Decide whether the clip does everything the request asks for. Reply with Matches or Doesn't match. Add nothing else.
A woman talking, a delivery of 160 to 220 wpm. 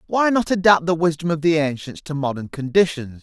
Doesn't match